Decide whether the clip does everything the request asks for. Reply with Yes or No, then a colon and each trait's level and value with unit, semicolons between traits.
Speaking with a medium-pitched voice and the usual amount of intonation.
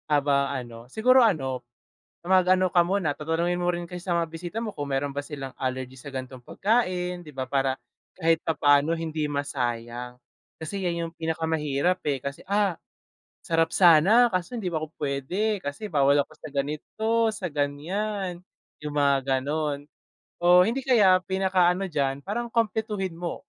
Yes: medium, 165 Hz; average, 4.8 semitones